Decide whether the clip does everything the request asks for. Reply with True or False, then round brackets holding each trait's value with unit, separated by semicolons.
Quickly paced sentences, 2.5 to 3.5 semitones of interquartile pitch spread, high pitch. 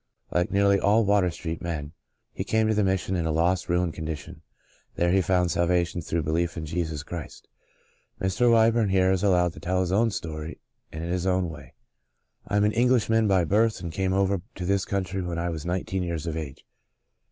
False (210 wpm; 2.8 semitones; 90 Hz)